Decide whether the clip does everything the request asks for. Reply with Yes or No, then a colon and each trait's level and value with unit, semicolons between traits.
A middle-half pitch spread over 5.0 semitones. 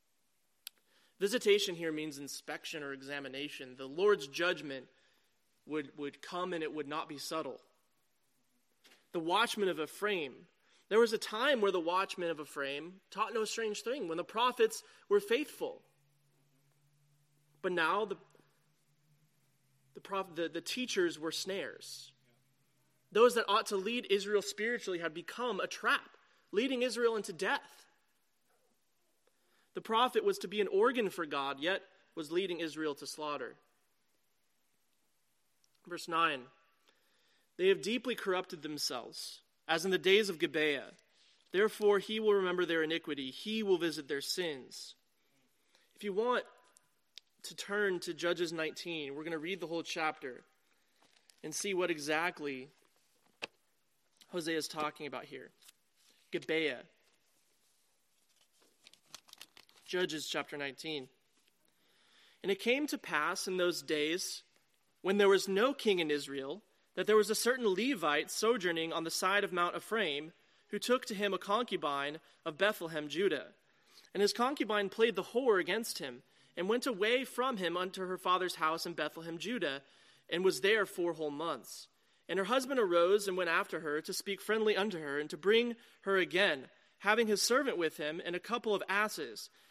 Yes: wide, 5.4 semitones